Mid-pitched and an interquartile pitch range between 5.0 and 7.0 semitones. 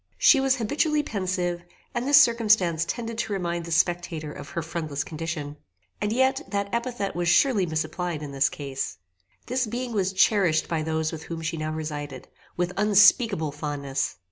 Yes: medium, 175 Hz; wide, 5.6 semitones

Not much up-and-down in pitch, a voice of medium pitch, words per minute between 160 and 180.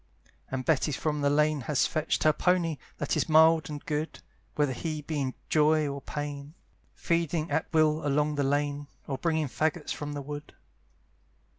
Yes: narrow, 1.6 semitones; medium, 150 Hz; average, 170 wpm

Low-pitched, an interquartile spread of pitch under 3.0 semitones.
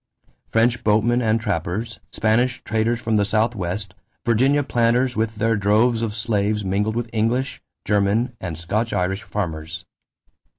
Yes: low, 110 Hz; narrow, 2.5 semitones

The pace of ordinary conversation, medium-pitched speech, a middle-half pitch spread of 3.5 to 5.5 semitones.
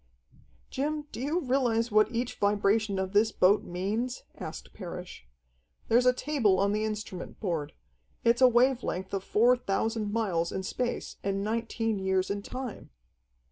No: average, 155 wpm; high, 215 Hz; average, 3.8 semitones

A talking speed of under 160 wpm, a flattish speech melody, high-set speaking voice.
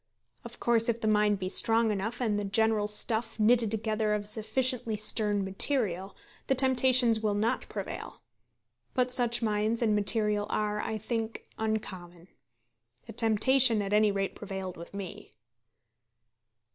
Yes: average, 145 wpm; narrow, 2.0 semitones; high, 215 Hz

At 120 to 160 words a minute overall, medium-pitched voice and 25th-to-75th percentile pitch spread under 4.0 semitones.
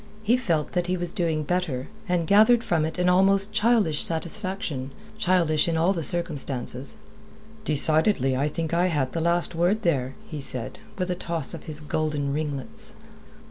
No: average, 170 wpm; medium, 165 Hz; average, 3.4 semitones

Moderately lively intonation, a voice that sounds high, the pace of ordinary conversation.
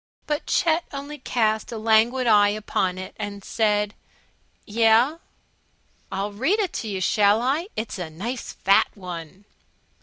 Yes: average, 4.0 semitones; high, 220 Hz; average, 145 wpm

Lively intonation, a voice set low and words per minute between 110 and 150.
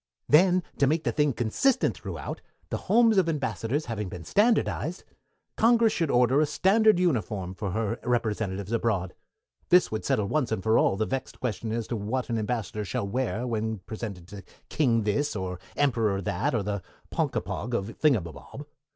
No: wide, 6.2 semitones; low, 115 Hz; average, 170 wpm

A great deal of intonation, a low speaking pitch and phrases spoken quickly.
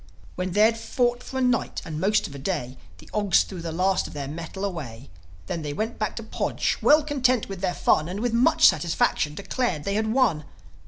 No: wide, 6.6 semitones; high, 195 Hz; fast, 220 wpm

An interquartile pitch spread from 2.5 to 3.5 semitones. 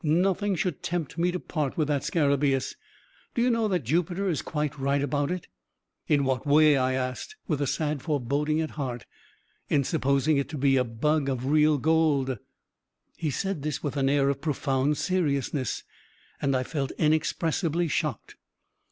Yes: average, 2.8 semitones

